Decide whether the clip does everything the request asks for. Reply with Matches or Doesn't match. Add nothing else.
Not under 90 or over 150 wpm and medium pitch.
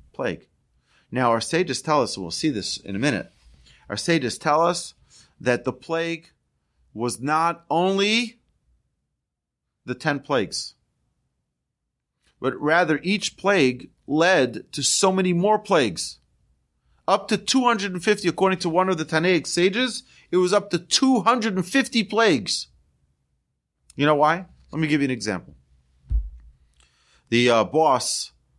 Matches